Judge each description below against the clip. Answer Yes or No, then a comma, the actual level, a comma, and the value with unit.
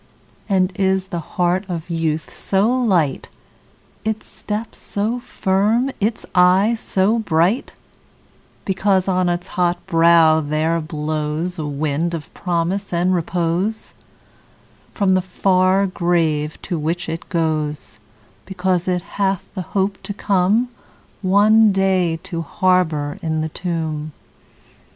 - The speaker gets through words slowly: Yes, slow, 125 wpm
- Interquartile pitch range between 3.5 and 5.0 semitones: No, average, 3.0 semitones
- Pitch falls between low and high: Yes, medium, 180 Hz